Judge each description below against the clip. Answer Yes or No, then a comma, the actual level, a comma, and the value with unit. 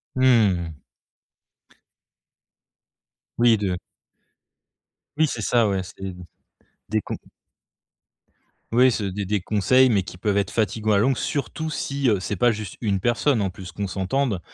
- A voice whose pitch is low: Yes, low, 105 Hz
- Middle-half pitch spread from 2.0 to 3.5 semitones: No, average, 3.9 semitones